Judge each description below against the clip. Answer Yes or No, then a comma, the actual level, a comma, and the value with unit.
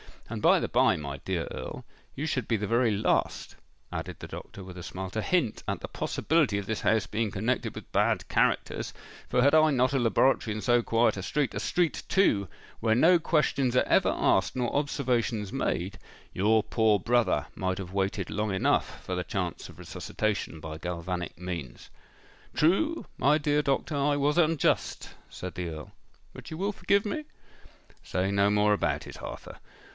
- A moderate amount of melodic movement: No, wide, 6.9 semitones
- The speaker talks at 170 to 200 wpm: Yes, average, 180 wpm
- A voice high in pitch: No, low, 110 Hz